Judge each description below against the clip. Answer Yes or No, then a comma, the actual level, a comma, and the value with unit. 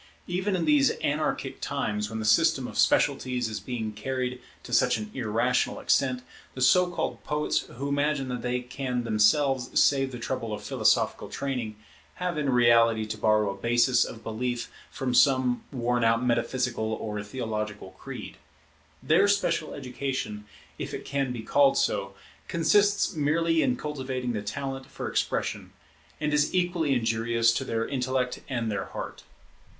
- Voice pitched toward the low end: Yes, low, 125 Hz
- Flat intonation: No, average, 3.9 semitones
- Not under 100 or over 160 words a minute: Yes, average, 155 wpm